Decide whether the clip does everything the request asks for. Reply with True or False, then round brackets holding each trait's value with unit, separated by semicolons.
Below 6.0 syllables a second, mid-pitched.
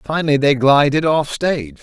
True (5.0 syllables/s; 145 Hz)